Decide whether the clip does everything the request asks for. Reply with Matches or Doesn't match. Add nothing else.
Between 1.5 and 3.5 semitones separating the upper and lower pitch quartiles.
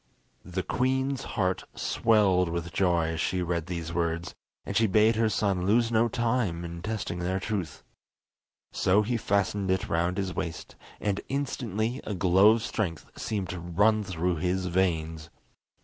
Doesn't match